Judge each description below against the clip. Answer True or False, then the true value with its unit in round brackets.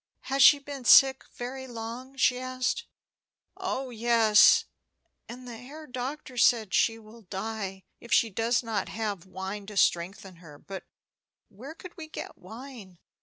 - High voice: True (235 Hz)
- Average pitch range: True (4.2 semitones)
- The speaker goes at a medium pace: True (150 wpm)